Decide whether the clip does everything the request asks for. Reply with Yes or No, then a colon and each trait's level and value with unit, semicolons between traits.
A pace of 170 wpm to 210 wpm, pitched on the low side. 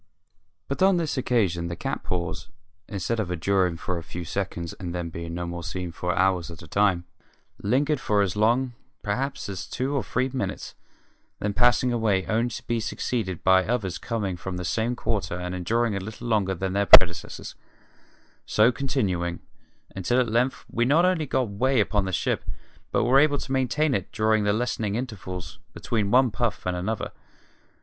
Yes: average, 185 wpm; low, 105 Hz